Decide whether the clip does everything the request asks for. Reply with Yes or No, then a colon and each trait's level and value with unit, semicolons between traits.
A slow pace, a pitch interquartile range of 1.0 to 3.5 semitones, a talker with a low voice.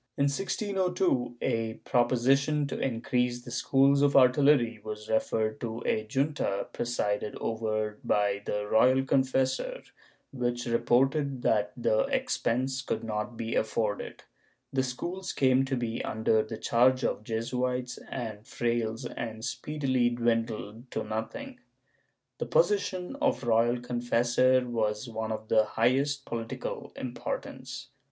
Yes: slow, 125 wpm; average, 3.2 semitones; low, 120 Hz